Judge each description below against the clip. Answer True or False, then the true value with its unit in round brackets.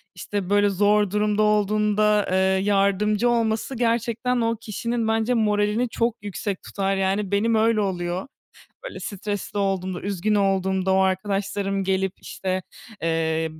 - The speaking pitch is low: False (205 Hz)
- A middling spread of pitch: False (1.9 semitones)